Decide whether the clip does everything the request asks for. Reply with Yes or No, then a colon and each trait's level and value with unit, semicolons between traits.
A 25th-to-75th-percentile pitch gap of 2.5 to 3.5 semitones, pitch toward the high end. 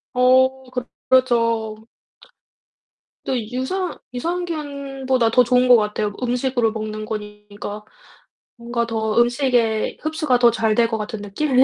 Yes: average, 3.0 semitones; high, 240 Hz